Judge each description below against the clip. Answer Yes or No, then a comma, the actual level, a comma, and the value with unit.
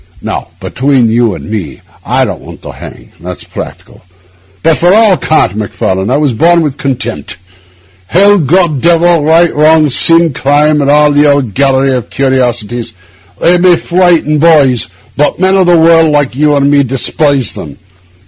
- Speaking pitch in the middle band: Yes, medium, 145 Hz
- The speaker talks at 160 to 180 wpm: Yes, average, 165 wpm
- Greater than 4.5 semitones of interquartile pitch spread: Yes, average, 4.9 semitones